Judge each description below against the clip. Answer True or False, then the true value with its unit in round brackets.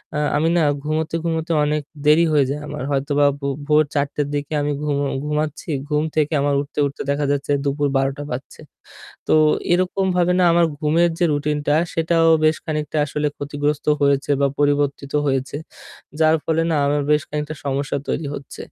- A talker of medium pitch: True (150 Hz)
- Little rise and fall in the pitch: True (1.7 semitones)